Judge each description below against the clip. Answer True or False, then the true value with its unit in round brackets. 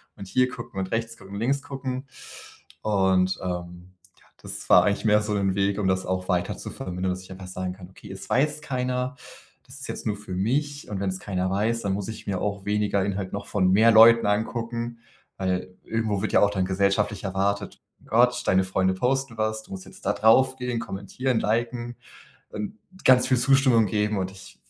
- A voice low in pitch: True (105 Hz)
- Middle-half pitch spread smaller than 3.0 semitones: False (3.9 semitones)